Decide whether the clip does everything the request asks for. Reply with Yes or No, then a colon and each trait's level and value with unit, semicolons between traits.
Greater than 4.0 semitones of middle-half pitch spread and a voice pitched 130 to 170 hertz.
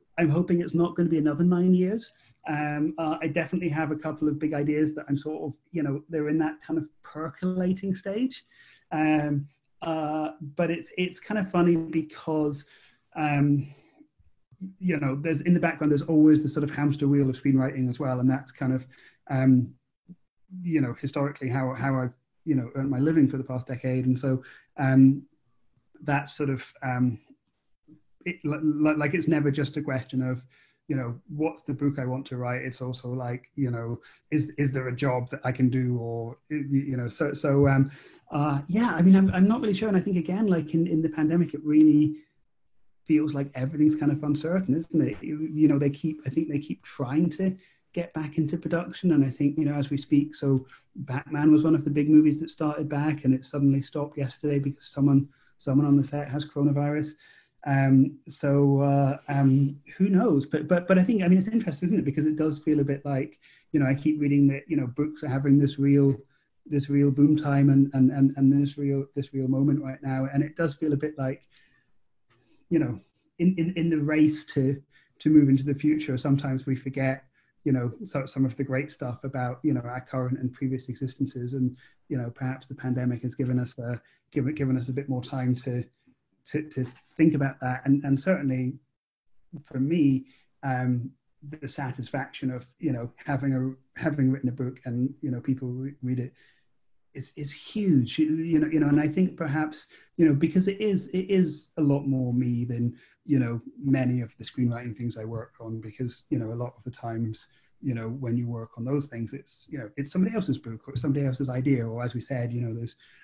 No: average, 2.8 semitones; medium, 140 Hz